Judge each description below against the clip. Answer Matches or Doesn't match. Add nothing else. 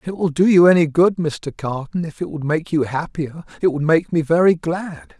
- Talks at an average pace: Doesn't match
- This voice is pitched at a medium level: Matches